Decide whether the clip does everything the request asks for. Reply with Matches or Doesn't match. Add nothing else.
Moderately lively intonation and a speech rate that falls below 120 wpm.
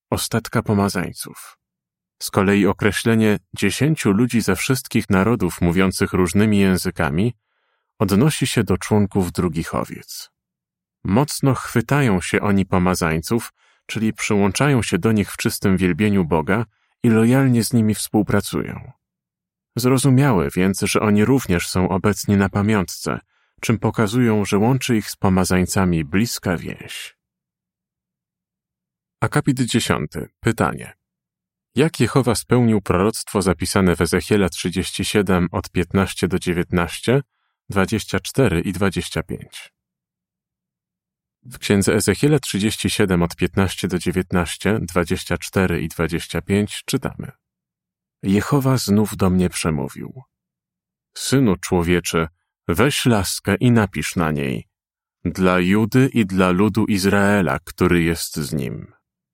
Matches